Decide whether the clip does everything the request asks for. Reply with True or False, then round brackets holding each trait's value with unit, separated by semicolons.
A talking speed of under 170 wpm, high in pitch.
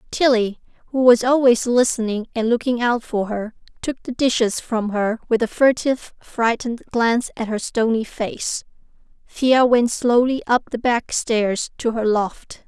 True (160 wpm; 235 Hz)